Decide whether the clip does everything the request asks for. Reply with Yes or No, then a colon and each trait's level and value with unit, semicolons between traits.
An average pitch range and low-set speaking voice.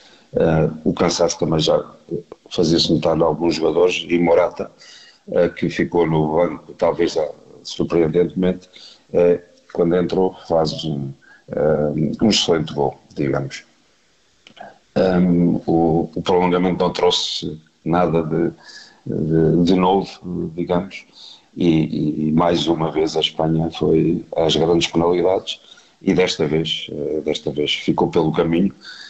No: narrow, 2.1 semitones; very low, 85 Hz